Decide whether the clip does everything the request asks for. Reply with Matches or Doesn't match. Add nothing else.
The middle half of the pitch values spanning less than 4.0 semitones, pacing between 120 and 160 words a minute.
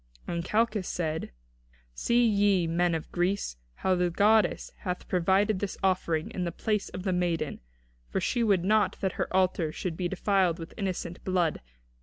Doesn't match